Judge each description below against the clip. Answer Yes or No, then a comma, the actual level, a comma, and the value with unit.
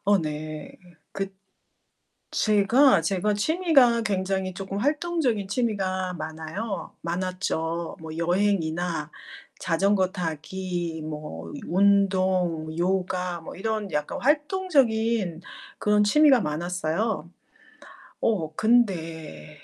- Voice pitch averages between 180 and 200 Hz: Yes, high, 190 Hz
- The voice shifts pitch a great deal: No, average, 4.5 semitones